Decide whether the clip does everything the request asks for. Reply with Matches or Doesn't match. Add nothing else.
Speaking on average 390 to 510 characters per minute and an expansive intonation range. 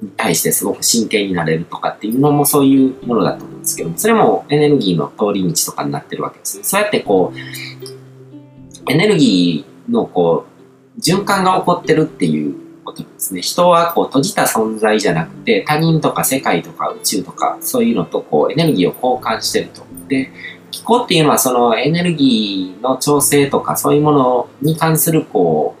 Matches